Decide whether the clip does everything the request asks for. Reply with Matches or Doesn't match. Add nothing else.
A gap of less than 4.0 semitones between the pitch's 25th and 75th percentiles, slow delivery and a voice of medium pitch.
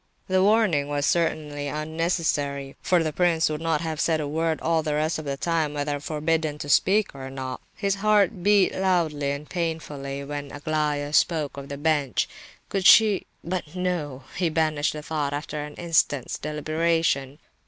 Doesn't match